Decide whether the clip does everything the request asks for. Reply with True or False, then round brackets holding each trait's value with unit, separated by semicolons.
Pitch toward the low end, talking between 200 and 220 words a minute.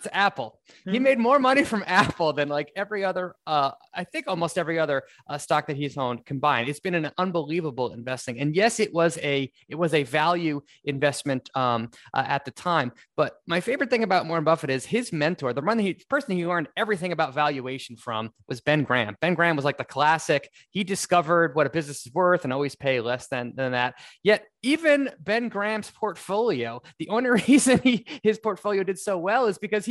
False (165 Hz; 205 wpm)